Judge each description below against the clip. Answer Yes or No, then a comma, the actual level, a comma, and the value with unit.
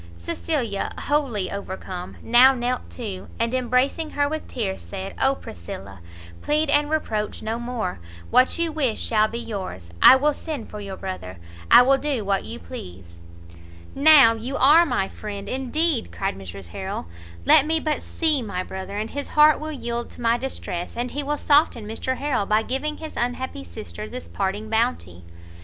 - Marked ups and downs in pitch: Yes, wide, 6.6 semitones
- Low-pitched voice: No, high, 235 Hz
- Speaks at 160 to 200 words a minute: Yes, average, 175 wpm